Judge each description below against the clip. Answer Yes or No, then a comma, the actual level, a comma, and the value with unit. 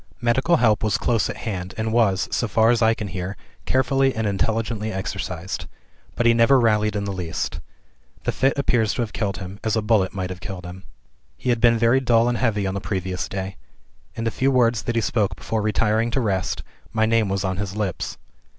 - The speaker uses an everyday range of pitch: Yes, average, 3.2 semitones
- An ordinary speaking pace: No, fast, 215 wpm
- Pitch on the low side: Yes, low, 110 Hz